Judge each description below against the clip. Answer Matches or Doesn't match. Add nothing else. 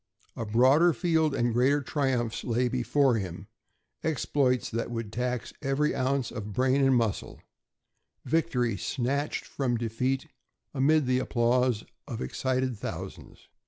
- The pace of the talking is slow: Matches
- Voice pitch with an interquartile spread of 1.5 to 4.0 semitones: Matches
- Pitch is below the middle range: Matches